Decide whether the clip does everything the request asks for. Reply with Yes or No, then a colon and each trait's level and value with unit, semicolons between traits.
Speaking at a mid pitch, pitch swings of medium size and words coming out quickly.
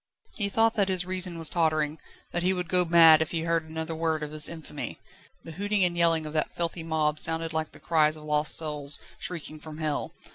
No: medium, 160 Hz; narrow, 2.0 semitones; fast, 220 wpm